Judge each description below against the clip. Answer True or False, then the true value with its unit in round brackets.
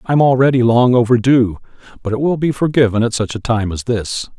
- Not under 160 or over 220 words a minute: True (205 wpm)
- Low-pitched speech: True (120 Hz)